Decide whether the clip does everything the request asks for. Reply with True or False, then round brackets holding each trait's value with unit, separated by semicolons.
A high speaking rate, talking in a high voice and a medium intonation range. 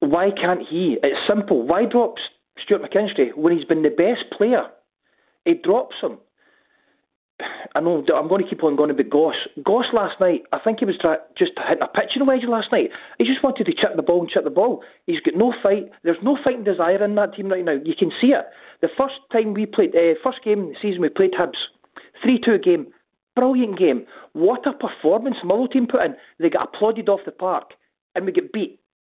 False (215 wpm; 210 Hz; 6.1 semitones)